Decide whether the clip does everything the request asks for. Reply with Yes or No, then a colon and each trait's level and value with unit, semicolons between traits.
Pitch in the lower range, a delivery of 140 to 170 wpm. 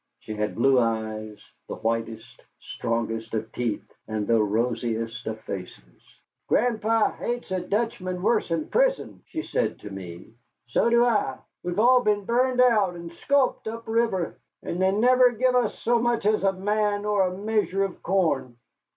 No: medium, 185 Hz; average, 160 wpm